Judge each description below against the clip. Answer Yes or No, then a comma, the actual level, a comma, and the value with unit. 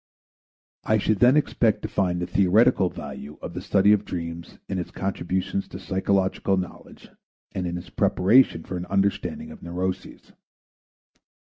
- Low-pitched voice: Yes, very low, 95 Hz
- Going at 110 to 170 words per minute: Yes, average, 150 wpm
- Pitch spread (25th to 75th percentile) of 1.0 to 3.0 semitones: Yes, narrow, 2.6 semitones